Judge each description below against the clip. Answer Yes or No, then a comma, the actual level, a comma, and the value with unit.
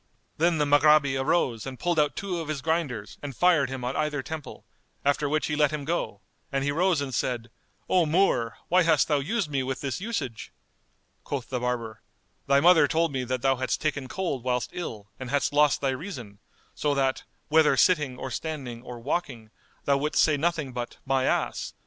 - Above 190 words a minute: Yes, average, 200 wpm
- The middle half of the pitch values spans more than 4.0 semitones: No, average, 3.6 semitones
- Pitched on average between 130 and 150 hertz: Yes, medium, 140 Hz